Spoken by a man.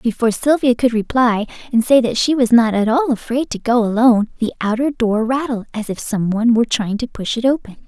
No: female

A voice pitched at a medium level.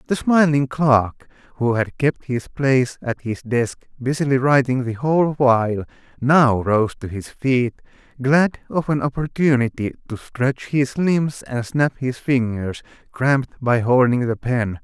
No: low, 130 Hz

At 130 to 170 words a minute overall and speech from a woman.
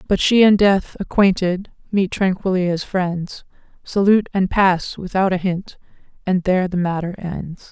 Yes: average, 155 wpm; female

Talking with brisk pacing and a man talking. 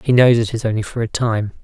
Yes: fast, 295 wpm; male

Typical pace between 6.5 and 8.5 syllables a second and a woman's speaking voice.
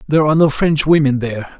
No: 7.0 syllables/s; male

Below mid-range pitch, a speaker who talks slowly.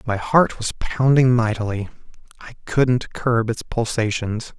Yes: low, 115 Hz; slow, 130 wpm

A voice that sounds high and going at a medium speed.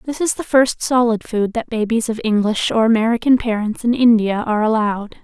Yes: high, 225 Hz; average, 195 wpm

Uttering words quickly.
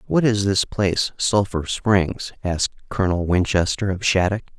No: average, 145 wpm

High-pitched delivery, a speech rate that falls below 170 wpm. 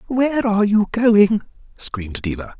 Yes: high, 195 Hz; average, 140 wpm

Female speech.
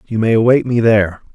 No: male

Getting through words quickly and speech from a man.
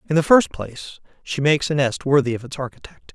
Yes: fast, 230 wpm; male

